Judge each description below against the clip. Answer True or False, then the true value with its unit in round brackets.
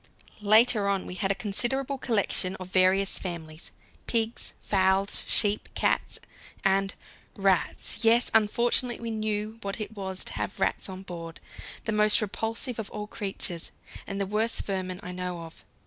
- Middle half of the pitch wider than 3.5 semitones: False (2.9 semitones)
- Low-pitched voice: False (200 Hz)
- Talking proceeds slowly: False (155 wpm)